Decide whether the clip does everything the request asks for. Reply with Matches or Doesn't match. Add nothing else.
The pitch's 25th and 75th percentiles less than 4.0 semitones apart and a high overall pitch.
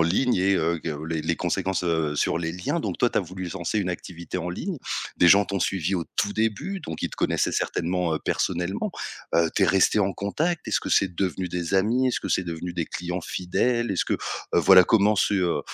Doesn't match